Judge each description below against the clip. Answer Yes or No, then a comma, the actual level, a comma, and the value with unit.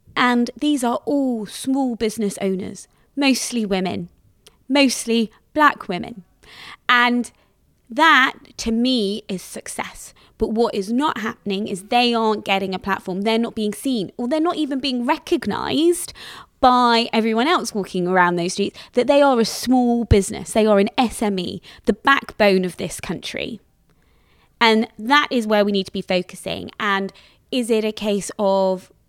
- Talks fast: No, average, 155 wpm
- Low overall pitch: No, high, 225 Hz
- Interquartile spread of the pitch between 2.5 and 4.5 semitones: Yes, average, 4.2 semitones